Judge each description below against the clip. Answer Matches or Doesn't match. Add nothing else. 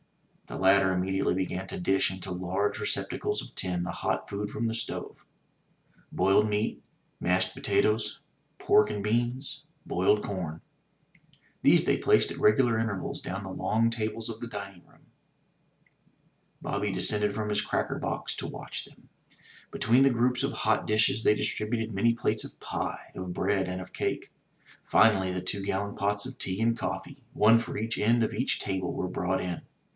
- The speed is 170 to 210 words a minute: Matches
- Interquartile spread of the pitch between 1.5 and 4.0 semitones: Matches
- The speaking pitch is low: Matches